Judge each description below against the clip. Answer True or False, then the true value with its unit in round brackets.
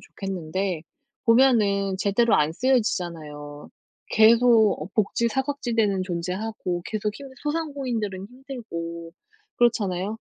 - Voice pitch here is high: True (210 Hz)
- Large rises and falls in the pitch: False (4.9 semitones)